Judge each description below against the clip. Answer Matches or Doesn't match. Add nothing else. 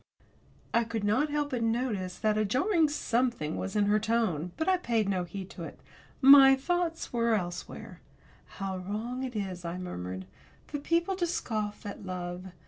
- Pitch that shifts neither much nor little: Doesn't match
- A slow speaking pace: Doesn't match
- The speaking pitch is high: Matches